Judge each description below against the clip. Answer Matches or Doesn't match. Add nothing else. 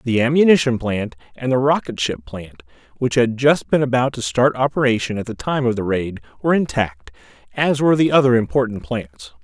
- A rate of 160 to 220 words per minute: Matches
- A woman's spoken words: Doesn't match